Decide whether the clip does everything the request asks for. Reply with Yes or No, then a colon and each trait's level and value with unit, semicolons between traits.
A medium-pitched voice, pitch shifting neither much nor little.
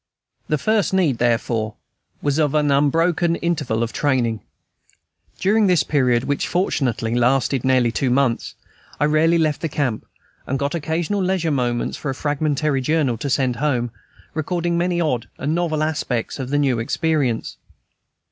Yes: medium, 145 Hz; average, 4.5 semitones